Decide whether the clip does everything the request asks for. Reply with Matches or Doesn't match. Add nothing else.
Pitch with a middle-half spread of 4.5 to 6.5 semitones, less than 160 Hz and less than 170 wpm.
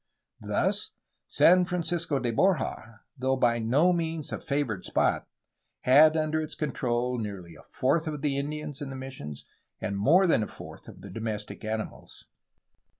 Matches